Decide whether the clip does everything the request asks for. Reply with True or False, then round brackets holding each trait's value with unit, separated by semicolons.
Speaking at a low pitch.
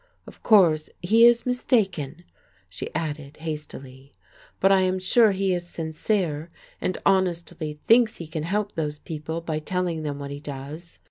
False (165 Hz)